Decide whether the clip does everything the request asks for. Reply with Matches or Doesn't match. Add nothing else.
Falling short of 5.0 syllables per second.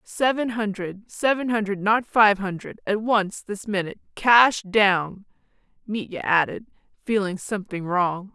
Matches